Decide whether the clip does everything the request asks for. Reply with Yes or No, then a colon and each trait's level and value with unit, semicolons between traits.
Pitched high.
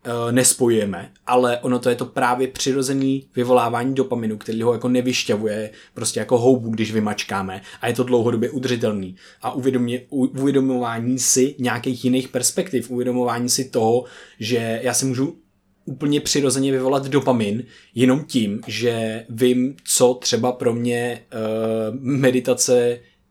No: low, 125 Hz